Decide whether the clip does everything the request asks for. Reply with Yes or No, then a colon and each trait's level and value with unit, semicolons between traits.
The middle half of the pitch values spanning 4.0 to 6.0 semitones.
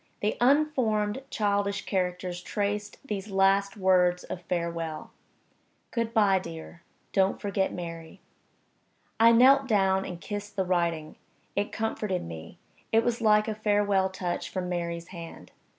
No: average, 3.0 semitones